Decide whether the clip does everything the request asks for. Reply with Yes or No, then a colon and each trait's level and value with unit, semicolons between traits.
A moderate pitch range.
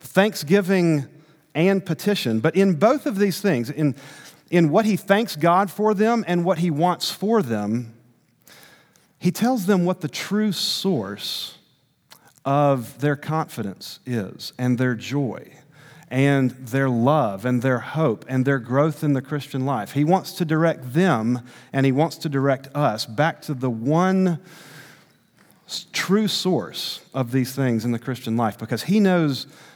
No: wide, 5.7 semitones